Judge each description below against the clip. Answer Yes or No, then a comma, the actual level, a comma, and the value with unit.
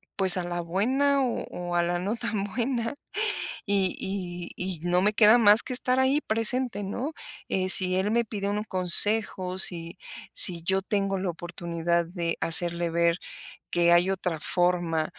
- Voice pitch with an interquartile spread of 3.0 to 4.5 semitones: Yes, average, 3.6 semitones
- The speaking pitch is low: No, high, 190 Hz